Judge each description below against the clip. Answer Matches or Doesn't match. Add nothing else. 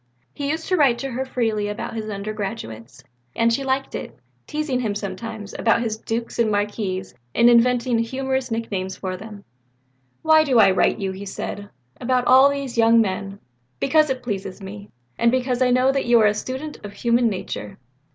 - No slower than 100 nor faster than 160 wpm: Doesn't match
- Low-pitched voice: Doesn't match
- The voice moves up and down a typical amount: Matches